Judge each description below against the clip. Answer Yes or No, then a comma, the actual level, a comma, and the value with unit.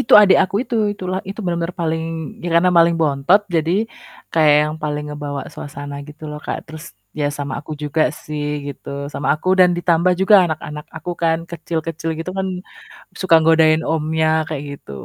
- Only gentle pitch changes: Yes, narrow, 2.3 semitones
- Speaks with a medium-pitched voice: Yes, medium, 160 Hz